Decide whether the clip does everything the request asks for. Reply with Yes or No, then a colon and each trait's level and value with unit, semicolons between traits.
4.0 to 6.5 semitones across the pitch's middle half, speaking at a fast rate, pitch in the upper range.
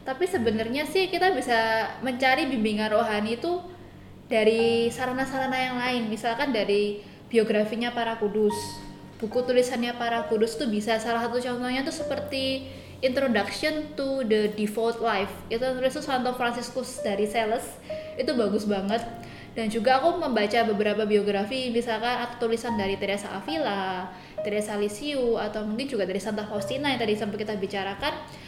No: average, 3.5 semitones; fast, 145 wpm; high, 230 Hz